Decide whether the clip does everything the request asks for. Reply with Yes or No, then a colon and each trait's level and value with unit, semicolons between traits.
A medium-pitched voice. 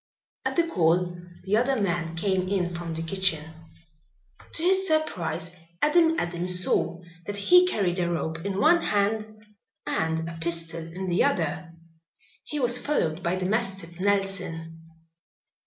Yes: medium, 180 Hz